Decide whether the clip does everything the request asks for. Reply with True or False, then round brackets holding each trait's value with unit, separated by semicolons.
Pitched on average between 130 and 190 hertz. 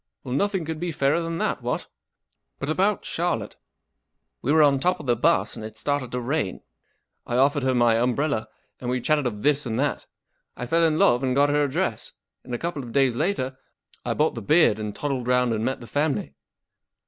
True (135 Hz)